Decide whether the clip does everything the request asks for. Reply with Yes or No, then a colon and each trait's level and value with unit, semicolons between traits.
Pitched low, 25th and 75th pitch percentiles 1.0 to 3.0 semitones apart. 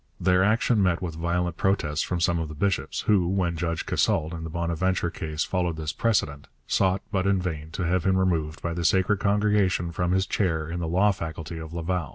Yes: very low, 85 Hz; narrow, 2.4 semitones